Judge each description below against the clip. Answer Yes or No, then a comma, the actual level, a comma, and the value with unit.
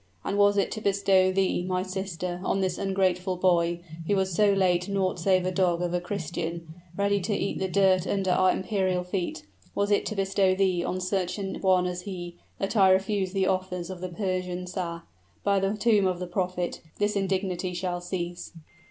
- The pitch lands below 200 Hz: Yes, medium, 185 Hz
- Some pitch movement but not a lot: No, narrow, 1.5 semitones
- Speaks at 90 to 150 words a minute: No, average, 195 wpm